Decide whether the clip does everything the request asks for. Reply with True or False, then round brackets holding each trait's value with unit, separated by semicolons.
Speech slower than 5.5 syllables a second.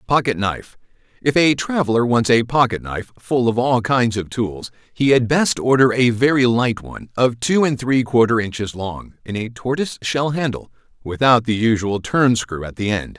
True (5.0 syllables/s)